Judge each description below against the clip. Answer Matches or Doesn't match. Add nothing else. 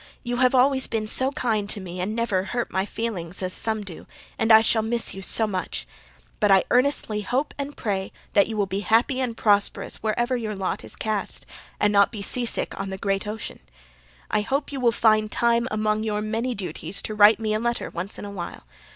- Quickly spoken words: Matches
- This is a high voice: Matches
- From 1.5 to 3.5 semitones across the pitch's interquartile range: Matches